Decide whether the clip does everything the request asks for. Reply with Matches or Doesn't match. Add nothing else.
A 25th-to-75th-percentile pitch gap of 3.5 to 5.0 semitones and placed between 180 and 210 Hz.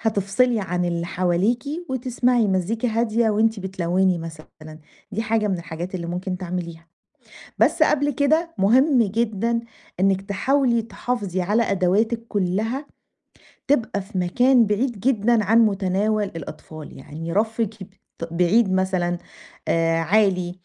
Matches